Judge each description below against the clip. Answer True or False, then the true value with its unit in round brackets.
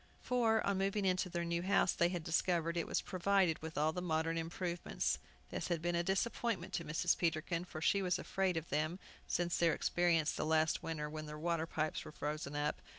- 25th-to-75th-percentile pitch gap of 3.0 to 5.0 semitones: False (2.5 semitones)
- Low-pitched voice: False (170 Hz)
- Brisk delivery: True (210 wpm)